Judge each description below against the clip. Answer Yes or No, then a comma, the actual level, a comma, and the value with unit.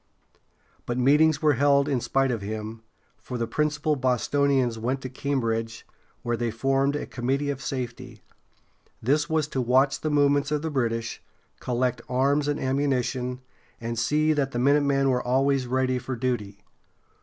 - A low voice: Yes, low, 130 Hz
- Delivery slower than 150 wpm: No, average, 155 wpm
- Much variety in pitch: No, average, 2.8 semitones